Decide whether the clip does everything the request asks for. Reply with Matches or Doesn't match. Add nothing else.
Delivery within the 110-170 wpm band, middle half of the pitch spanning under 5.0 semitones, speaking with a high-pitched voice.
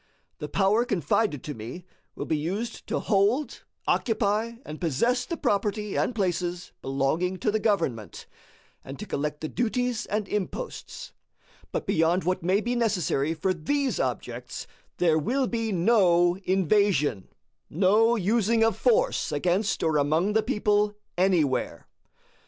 Doesn't match